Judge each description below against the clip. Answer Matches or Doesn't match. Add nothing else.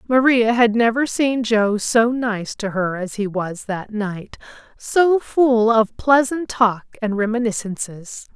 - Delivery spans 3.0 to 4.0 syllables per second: Matches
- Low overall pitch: Doesn't match